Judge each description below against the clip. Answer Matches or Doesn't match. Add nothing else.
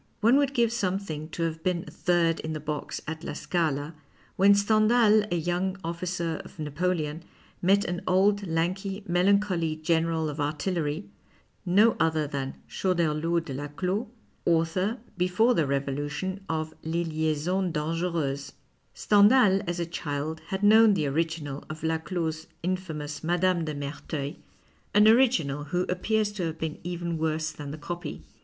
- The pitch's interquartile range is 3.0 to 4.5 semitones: Matches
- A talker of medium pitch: Matches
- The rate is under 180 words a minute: Matches